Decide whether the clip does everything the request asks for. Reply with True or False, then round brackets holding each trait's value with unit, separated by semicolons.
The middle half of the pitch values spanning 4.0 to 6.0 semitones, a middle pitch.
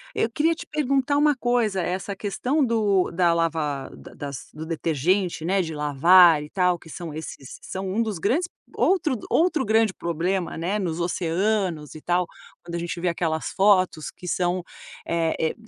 True (4.6 semitones; 180 Hz)